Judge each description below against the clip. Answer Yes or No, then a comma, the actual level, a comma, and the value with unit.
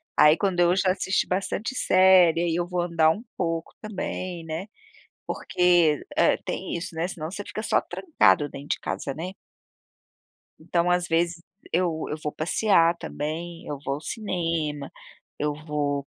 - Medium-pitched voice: Yes, medium, 170 Hz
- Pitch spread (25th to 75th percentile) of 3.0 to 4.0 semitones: No, narrow, 2.5 semitones